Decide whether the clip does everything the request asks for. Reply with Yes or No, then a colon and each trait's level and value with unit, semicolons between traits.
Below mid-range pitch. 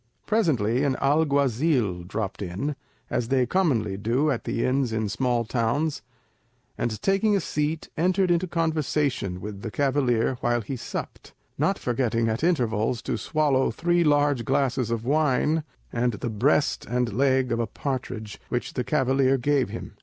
Yes: low, 130 Hz